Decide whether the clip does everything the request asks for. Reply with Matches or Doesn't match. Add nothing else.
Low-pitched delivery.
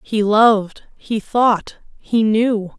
Doesn't match